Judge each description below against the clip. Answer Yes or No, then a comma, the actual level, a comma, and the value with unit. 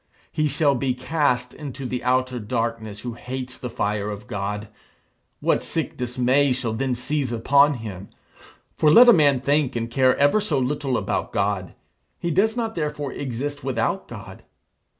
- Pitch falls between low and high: No, low, 130 Hz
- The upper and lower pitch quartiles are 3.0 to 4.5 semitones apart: Yes, average, 3.6 semitones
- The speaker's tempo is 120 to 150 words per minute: No, average, 165 wpm